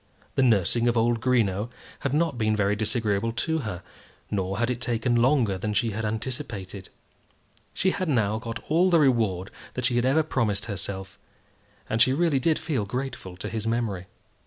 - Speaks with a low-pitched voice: Yes, low, 115 Hz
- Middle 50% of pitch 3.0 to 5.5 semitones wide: Yes, average, 4.0 semitones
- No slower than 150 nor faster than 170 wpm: No, average, 180 wpm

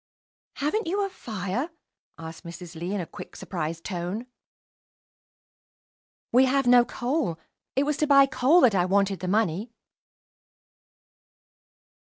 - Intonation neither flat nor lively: No, wide, 7.5 semitones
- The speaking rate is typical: No, slow, 130 wpm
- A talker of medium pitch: No, high, 215 Hz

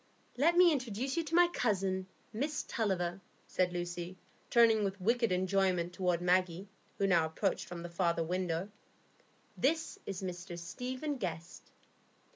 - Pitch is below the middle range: No, high, 190 Hz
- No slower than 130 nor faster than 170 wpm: Yes, average, 140 wpm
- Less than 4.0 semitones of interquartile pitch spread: No, average, 5.2 semitones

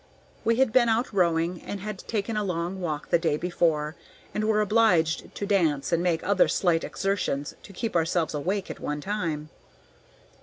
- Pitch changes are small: No, average, 4.2 semitones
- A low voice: No, medium, 180 Hz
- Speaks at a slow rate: No, average, 180 wpm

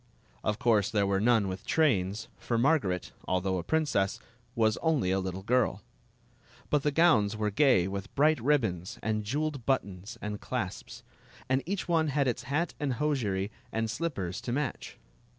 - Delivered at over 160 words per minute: Yes, average, 170 wpm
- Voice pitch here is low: Yes, low, 115 Hz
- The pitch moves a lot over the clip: Yes, wide, 6.8 semitones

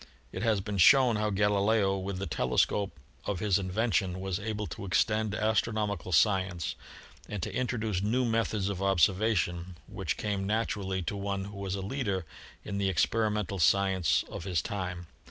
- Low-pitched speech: Yes, low, 100 Hz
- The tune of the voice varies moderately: No, narrow, 2.2 semitones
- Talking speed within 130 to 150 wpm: No, average, 165 wpm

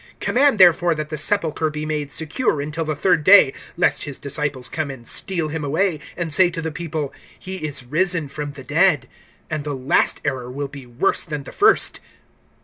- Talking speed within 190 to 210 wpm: Yes, average, 195 wpm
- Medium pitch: Yes, medium, 155 Hz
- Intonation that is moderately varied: Yes, average, 3.2 semitones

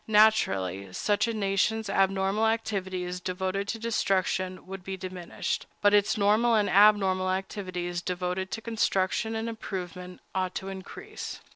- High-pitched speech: Yes, high, 195 Hz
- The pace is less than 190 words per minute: Yes, slow, 135 wpm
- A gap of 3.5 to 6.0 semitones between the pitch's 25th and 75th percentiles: No, narrow, 2.4 semitones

